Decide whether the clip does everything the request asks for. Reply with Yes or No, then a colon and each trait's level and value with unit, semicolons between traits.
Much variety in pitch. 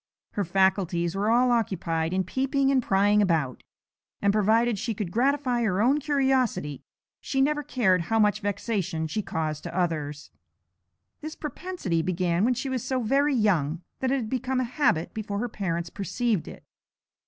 Yes: wide, 6.2 semitones